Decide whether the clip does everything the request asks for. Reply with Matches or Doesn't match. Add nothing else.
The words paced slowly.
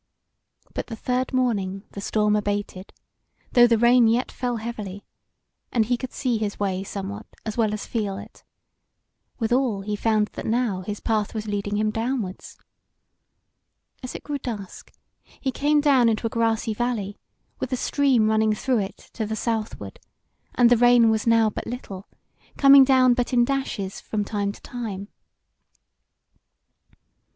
Doesn't match